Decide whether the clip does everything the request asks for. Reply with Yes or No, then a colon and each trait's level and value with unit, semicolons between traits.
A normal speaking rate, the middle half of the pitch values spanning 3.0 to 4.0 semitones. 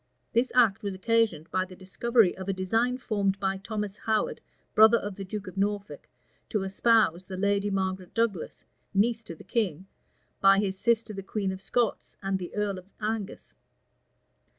No: average, 175 wpm; narrow, 2.6 semitones